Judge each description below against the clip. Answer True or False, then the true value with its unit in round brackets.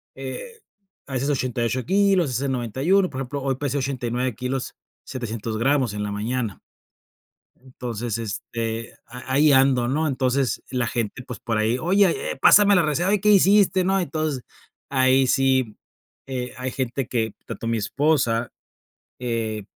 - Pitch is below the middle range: True (130 Hz)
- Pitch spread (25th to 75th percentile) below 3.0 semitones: False (3.8 semitones)